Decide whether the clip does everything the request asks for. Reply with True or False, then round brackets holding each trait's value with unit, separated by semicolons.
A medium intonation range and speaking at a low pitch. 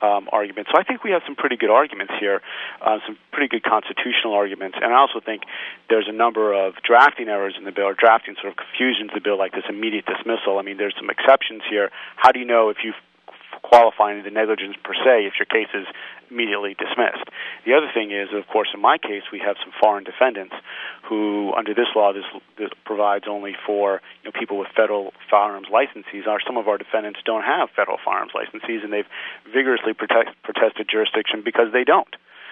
False (1.7 semitones; 105 Hz)